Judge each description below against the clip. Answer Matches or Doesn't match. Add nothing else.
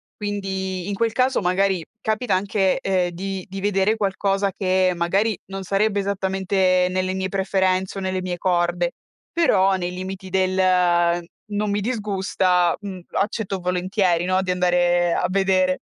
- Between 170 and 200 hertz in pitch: Matches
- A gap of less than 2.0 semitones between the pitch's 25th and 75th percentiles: Matches